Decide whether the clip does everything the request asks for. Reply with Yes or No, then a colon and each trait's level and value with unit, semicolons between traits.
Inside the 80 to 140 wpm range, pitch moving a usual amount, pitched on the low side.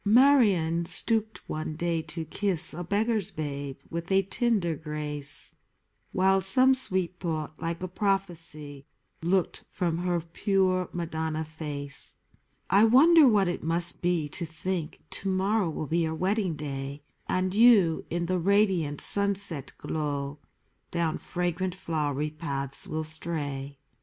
No: slow, 135 wpm; average, 3.8 semitones; medium, 170 Hz